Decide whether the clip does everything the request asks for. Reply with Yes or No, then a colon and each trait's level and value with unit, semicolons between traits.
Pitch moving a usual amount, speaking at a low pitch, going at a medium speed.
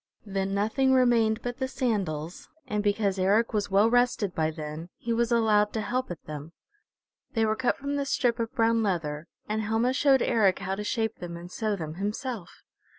No: average, 3.8 semitones; high, 215 Hz; average, 195 wpm